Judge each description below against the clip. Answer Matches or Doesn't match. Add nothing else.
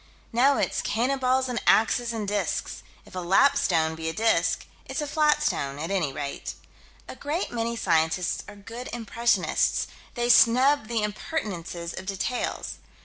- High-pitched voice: Matches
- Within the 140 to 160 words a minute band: Matches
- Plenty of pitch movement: Matches